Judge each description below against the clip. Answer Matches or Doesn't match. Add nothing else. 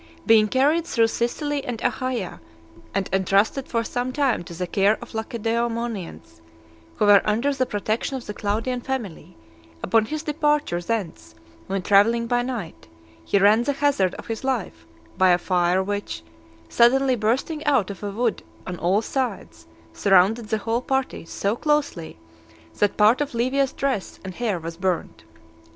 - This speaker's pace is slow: Doesn't match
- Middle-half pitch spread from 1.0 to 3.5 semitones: Doesn't match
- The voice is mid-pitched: Doesn't match